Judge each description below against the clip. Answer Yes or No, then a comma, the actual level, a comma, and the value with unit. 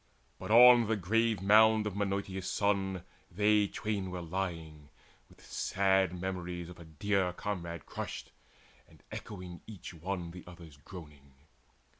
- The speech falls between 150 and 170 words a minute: No, slow, 135 wpm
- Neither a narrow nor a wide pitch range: Yes, average, 3.0 semitones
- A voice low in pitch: Yes, very low, 95 Hz